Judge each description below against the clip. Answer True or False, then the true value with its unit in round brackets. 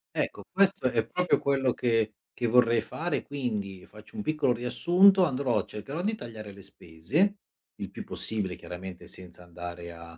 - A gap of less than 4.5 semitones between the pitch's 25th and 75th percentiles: False (8.2 semitones)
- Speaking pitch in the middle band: False (115 Hz)